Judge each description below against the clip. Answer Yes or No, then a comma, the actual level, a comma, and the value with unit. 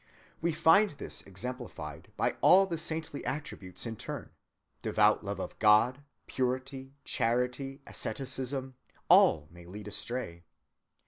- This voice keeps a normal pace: No, slow, 115 wpm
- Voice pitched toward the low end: Yes, low, 130 Hz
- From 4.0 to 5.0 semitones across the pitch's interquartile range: Yes, average, 4.3 semitones